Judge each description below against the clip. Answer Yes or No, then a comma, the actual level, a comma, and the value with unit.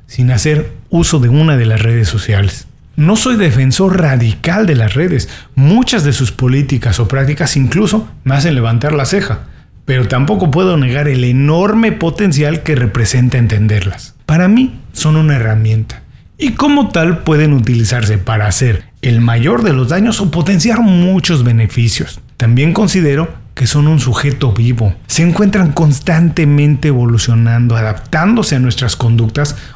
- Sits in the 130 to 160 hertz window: Yes, low, 135 Hz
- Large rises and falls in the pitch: Yes, wide, 6.1 semitones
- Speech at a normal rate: Yes, average, 150 wpm